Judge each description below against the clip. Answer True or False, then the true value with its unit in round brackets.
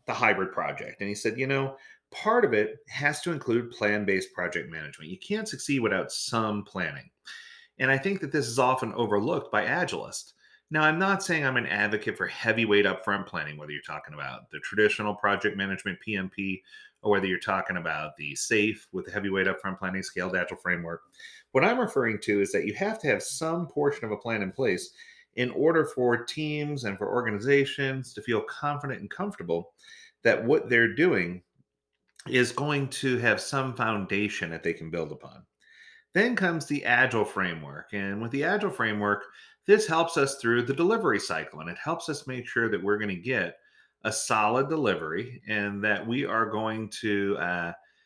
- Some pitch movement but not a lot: False (5.8 semitones)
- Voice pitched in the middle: False (115 Hz)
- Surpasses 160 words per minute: True (190 wpm)